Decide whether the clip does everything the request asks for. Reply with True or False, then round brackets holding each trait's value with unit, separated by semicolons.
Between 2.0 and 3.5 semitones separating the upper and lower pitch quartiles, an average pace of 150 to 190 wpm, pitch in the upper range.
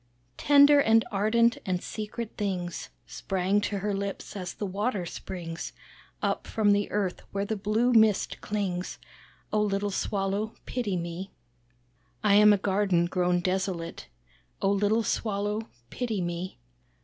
False (2.4 semitones; 135 wpm; 200 Hz)